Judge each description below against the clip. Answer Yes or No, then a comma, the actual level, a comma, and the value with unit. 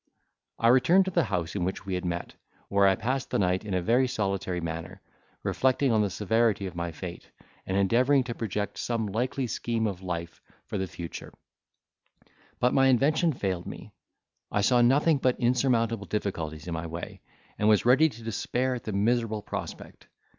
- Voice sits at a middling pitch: No, low, 110 Hz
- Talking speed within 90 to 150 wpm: No, average, 180 wpm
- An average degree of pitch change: Yes, average, 5.0 semitones